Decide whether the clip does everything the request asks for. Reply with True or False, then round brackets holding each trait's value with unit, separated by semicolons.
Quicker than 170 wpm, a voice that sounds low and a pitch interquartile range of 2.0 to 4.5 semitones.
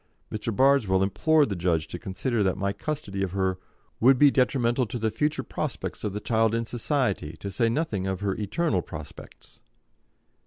False (180 wpm; 110 Hz; 5.0 semitones)